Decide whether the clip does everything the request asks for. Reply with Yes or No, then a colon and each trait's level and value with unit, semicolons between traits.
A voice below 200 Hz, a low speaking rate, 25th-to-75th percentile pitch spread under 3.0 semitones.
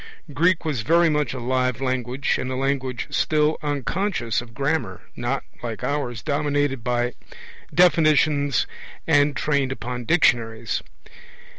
No: low, 135 Hz; slow, 125 wpm; average, 3.5 semitones